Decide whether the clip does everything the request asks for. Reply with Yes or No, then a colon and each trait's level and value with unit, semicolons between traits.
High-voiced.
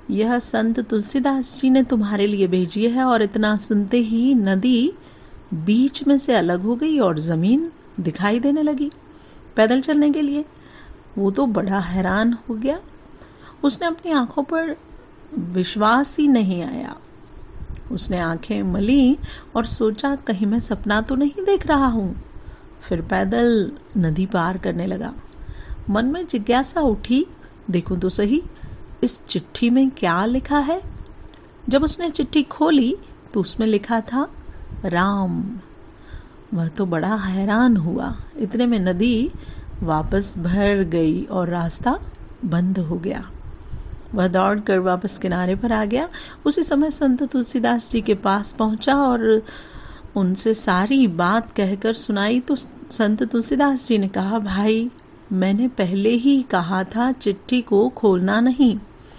Yes: high, 225 Hz